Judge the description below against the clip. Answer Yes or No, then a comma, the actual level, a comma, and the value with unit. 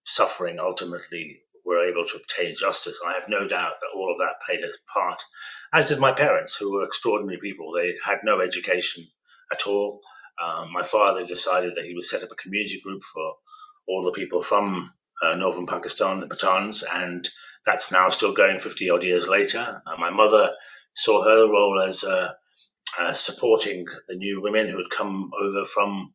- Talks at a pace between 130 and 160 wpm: No, average, 185 wpm